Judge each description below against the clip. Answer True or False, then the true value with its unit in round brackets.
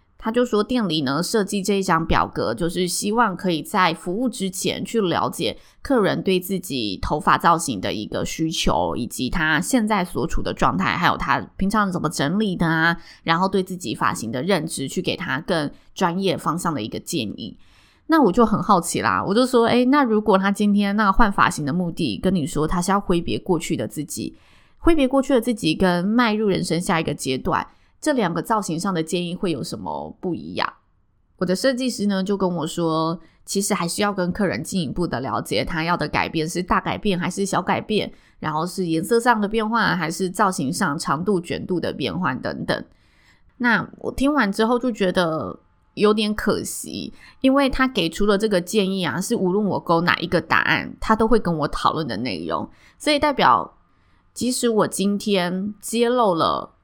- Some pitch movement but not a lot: True (4.5 semitones)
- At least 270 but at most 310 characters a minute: True (285 characters per minute)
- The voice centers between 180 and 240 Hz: True (190 Hz)